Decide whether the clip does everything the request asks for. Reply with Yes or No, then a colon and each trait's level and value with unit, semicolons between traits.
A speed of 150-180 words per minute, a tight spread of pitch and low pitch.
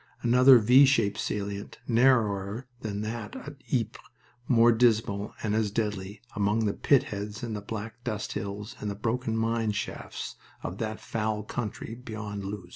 Yes: average, 160 wpm; narrow, 2.2 semitones; low, 110 Hz